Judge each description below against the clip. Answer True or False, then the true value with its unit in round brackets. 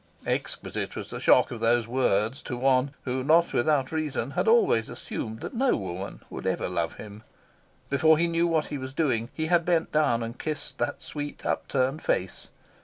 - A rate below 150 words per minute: False (185 wpm)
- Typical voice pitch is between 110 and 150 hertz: True (135 Hz)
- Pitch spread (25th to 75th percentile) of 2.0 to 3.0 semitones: False (5.2 semitones)